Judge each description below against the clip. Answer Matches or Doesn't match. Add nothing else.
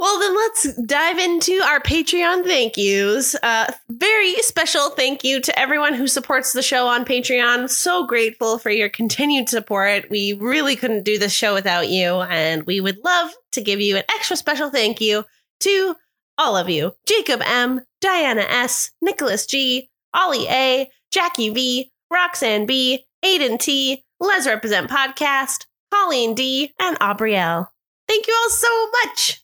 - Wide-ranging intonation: Matches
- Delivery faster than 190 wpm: Doesn't match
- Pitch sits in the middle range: Doesn't match